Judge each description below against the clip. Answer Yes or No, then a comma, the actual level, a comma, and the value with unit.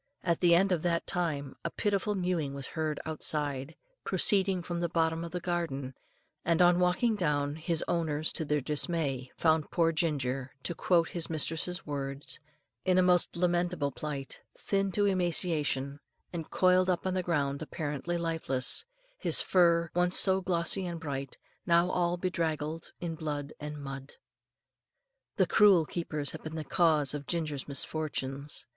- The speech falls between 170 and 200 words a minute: No, average, 160 wpm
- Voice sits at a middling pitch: Yes, medium, 165 Hz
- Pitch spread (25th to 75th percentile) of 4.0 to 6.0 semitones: No, average, 3.2 semitones